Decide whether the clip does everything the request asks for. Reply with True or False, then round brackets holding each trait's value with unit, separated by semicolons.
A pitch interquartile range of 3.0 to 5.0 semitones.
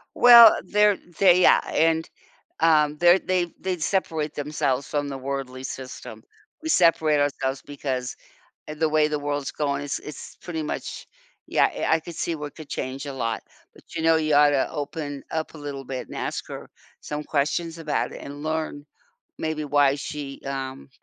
False (2.5 semitones)